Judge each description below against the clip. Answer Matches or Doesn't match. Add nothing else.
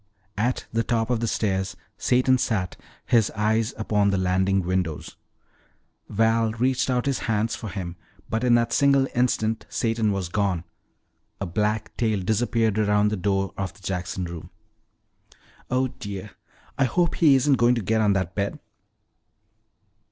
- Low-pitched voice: Matches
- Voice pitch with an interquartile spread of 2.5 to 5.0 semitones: Matches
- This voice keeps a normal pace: Matches